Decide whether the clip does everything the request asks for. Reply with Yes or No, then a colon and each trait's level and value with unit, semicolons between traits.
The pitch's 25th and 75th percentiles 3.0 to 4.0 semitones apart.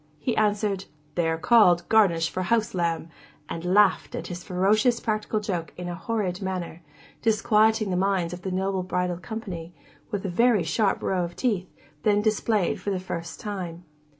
Yes: average, 3.3 semitones